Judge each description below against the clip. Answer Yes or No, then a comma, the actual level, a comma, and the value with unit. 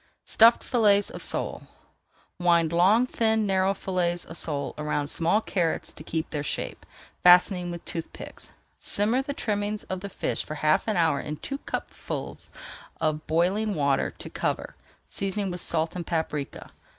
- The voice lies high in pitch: No, medium, 180 Hz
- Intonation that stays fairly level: No, average, 4.2 semitones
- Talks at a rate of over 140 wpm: Yes, average, 160 wpm